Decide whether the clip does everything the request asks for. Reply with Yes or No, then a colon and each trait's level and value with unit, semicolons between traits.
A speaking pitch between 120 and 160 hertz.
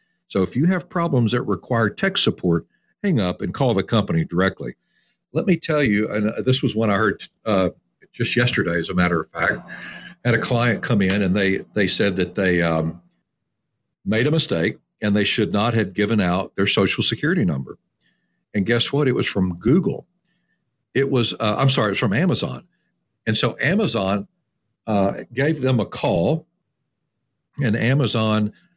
No: low, 110 Hz